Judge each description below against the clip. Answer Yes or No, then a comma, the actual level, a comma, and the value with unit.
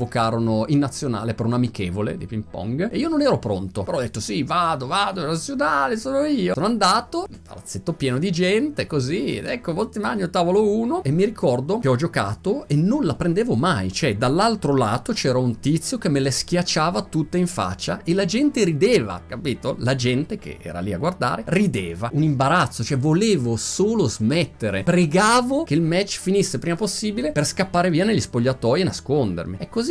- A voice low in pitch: No, medium, 165 Hz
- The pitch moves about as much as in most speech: No, wide, 7.9 semitones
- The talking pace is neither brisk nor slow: No, fast, 195 wpm